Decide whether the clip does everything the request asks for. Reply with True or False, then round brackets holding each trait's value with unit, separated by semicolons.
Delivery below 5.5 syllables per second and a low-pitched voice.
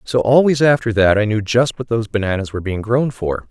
False (6.0 syllables/s; 115 Hz)